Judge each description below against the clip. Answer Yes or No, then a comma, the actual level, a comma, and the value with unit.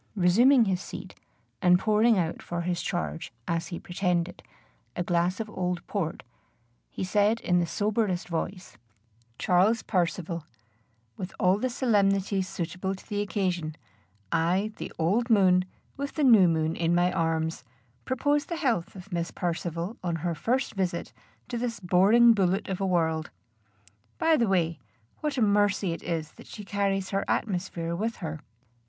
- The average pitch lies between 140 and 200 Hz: Yes, medium, 185 Hz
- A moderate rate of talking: Yes, average, 160 wpm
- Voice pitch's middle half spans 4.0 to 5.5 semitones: No, average, 3.5 semitones